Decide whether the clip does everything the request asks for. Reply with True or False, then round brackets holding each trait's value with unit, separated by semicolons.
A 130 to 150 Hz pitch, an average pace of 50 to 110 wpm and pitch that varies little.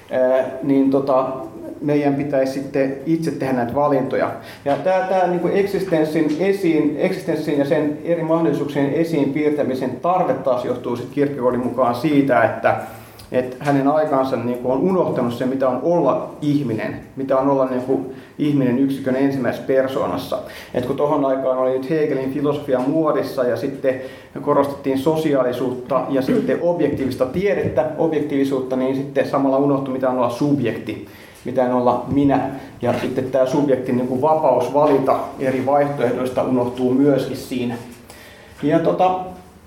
False (135 Hz; 135 wpm; 2.3 semitones)